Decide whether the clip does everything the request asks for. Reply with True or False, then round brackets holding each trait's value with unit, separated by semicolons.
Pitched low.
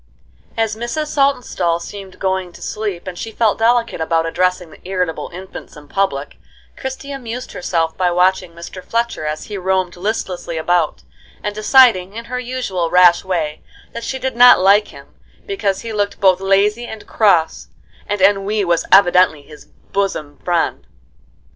False (190 Hz)